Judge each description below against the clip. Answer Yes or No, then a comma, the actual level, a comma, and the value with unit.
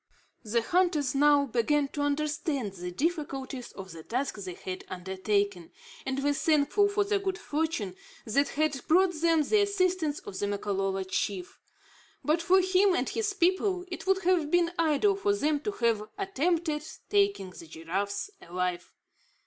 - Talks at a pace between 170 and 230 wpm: No, average, 155 wpm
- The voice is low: No, very high, 295 Hz